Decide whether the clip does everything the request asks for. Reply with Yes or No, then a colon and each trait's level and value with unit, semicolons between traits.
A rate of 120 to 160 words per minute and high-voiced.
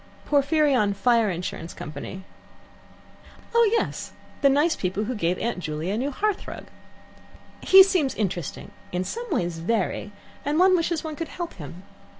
Yes: average, 155 wpm; high, 240 Hz